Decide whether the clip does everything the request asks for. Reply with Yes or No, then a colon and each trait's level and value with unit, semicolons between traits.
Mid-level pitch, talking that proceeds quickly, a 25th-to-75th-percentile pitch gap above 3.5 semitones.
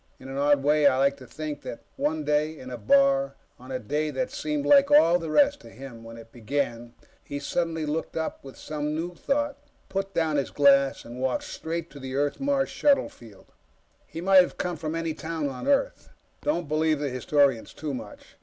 Yes: medium, 150 Hz; fast, 210 wpm; average, 4.3 semitones